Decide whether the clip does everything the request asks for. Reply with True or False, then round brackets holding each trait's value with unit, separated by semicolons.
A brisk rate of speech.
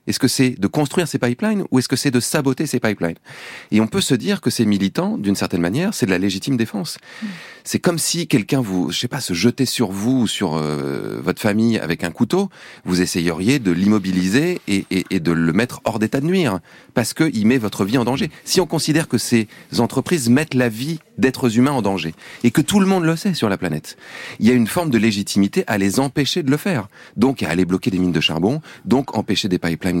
True (240 wpm)